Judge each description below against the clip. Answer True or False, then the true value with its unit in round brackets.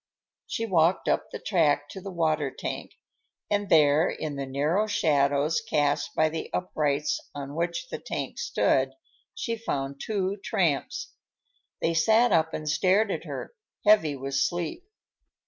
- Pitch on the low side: False (160 Hz)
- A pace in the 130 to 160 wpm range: True (145 wpm)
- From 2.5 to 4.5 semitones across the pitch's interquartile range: False (5.1 semitones)